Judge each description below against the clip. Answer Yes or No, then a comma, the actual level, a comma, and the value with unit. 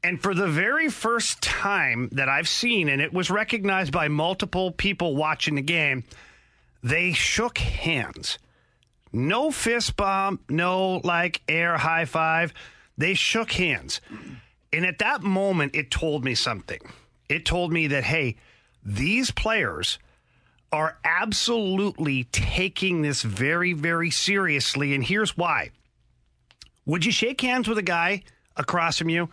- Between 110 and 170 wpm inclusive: Yes, average, 140 wpm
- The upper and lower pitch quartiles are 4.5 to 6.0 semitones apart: Yes, average, 5.1 semitones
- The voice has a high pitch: No, medium, 170 Hz